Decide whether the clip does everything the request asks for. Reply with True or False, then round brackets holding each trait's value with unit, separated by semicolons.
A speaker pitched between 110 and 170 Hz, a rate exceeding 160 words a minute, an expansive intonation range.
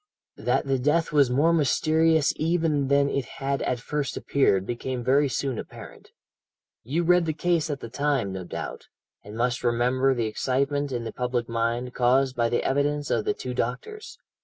False (135 Hz; 180 wpm; 3.4 semitones)